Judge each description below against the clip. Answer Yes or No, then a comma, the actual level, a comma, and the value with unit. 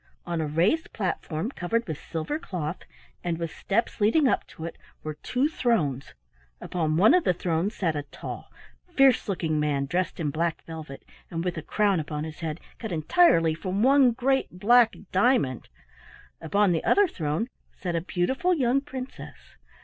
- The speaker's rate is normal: Yes, average, 170 wpm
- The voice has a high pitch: No, medium, 180 Hz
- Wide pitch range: Yes, wide, 7.1 semitones